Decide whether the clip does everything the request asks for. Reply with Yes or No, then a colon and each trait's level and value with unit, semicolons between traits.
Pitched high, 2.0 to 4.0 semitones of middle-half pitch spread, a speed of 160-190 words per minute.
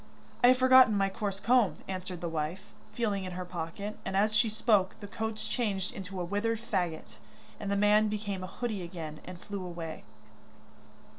Yes: high, 200 Hz; average, 2.9 semitones; average, 180 wpm